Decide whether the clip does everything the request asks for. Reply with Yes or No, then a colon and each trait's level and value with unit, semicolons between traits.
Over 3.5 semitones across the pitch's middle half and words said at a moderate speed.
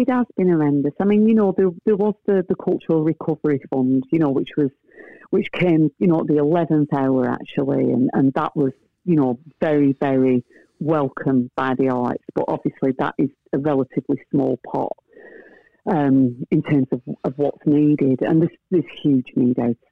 Yes: average, 4.7 semitones; average, 185 wpm